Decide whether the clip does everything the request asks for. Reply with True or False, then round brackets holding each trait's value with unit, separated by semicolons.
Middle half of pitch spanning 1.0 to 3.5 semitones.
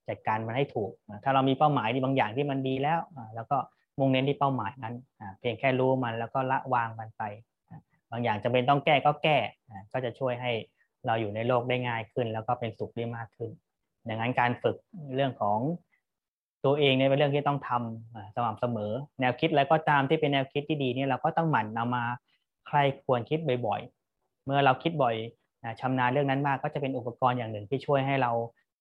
True (3.2 semitones)